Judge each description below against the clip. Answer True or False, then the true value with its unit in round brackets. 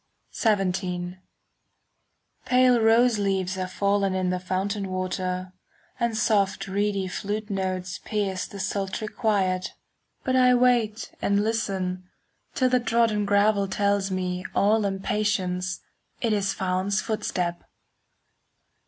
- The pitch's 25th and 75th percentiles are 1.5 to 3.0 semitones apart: True (2.5 semitones)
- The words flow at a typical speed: False (120 wpm)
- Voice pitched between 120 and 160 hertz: False (200 Hz)